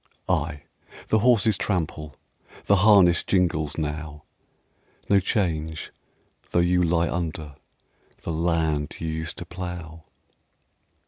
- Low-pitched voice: Yes, very low, 85 Hz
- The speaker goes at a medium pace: No, slow, 110 wpm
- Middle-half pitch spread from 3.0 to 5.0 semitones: No, narrow, 2.5 semitones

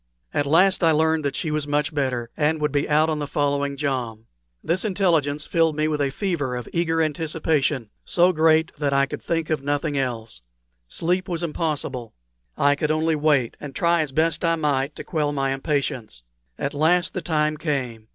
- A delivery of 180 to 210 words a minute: Yes, average, 190 wpm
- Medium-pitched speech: Yes, medium, 150 Hz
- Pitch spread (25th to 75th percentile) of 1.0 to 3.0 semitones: Yes, average, 2.7 semitones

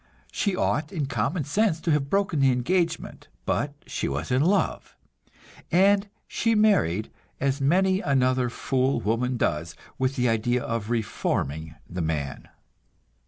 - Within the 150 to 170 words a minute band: No, average, 140 wpm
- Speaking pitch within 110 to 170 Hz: Yes, low, 135 Hz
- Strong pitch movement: Yes, wide, 7.1 semitones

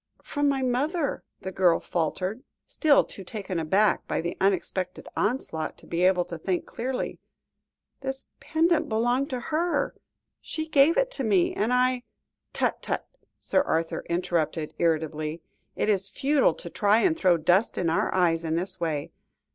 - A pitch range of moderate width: No, wide, 7.7 semitones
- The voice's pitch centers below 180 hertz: No, high, 195 Hz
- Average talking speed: Yes, average, 165 wpm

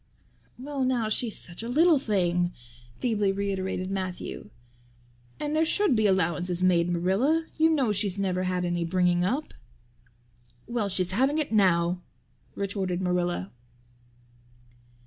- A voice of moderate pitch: No, high, 195 Hz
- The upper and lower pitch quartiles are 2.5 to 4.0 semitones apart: No, average, 5.3 semitones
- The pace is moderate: No, slow, 125 wpm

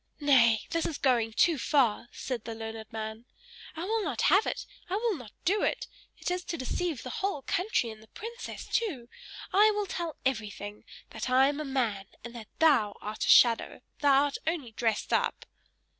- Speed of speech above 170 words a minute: Yes, average, 190 wpm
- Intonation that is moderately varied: No, wide, 7.3 semitones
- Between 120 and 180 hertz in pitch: No, very high, 265 Hz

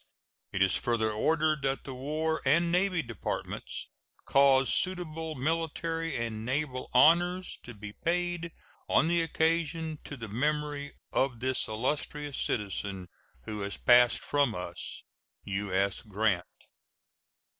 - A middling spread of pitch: No, wide, 6.6 semitones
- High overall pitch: No, medium, 140 Hz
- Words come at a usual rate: No, slow, 125 wpm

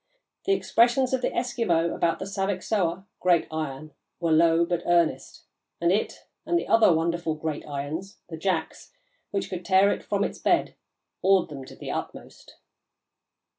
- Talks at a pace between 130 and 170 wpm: Yes, average, 160 wpm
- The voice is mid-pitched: Yes, medium, 175 Hz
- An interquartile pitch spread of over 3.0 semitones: Yes, average, 3.4 semitones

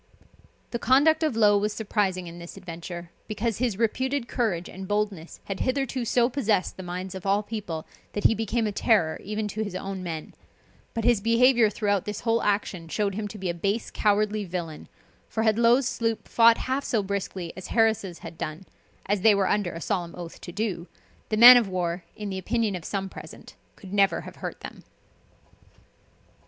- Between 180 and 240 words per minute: Yes, average, 195 wpm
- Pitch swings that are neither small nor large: Yes, average, 3.6 semitones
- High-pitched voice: Yes, high, 205 Hz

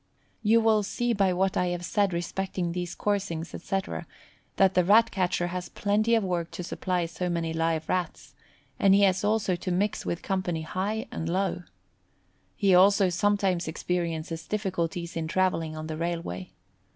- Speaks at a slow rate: No, average, 165 wpm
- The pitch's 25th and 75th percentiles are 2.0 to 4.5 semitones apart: Yes, average, 2.7 semitones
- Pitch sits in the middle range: Yes, medium, 180 Hz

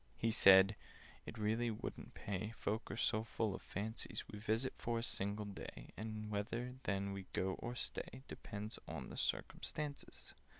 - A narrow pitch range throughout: Yes, narrow, 2.2 semitones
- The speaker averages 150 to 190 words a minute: Yes, average, 160 wpm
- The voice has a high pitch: No, low, 110 Hz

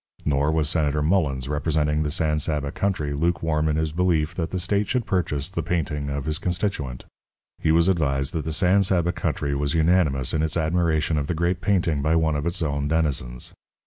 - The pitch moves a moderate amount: Yes, average, 3.0 semitones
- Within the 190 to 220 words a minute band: Yes, average, 200 wpm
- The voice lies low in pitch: Yes, very low, 80 Hz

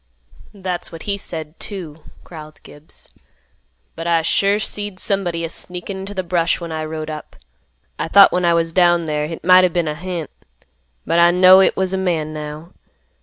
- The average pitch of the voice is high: No, medium, 170 Hz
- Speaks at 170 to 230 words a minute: Yes, average, 190 wpm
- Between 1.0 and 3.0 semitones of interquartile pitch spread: Yes, average, 2.7 semitones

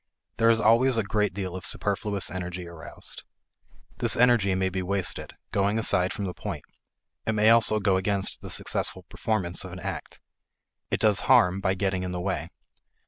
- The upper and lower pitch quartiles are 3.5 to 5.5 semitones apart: No, average, 2.8 semitones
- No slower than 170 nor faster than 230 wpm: Yes, average, 180 wpm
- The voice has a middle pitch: No, low, 100 Hz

